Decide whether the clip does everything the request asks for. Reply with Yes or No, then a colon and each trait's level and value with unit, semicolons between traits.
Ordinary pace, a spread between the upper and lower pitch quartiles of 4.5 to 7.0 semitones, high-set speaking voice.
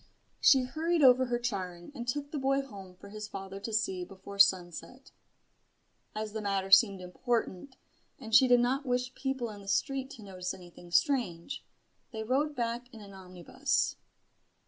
Yes: average, 170 wpm; average, 5.1 semitones; high, 220 Hz